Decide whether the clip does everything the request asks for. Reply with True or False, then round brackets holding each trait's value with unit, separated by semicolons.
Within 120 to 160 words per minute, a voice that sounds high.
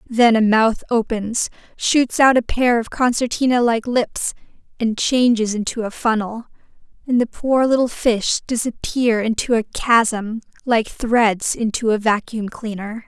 True (145 wpm; 230 Hz)